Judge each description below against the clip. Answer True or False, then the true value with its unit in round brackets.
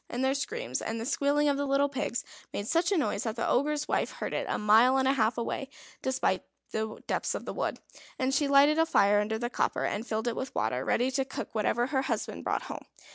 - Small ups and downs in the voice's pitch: False (3.9 semitones)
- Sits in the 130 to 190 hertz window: False (265 Hz)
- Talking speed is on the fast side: True (240 wpm)